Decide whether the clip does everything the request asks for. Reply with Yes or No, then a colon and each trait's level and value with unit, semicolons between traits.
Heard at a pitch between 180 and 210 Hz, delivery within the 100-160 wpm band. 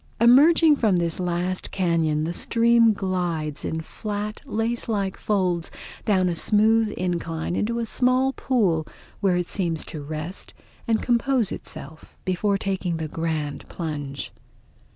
Yes: medium, 185 Hz; slow, 135 wpm